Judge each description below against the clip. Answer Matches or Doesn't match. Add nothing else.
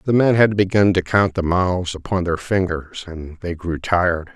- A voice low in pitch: Matches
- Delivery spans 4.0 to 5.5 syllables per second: Matches